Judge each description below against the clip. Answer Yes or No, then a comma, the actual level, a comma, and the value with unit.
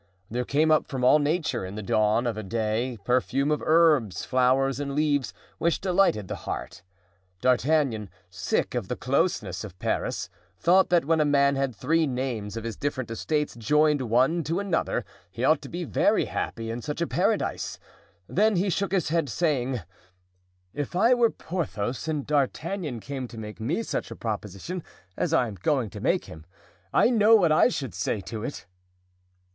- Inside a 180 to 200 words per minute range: Yes, average, 185 wpm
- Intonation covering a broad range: Yes, wide, 5.9 semitones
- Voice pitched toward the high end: No, low, 135 Hz